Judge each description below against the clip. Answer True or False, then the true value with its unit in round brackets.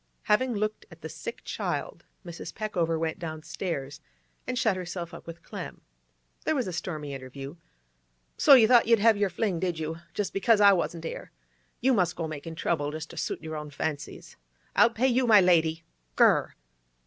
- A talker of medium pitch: True (175 Hz)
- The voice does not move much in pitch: False (5.1 semitones)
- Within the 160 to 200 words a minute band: True (190 wpm)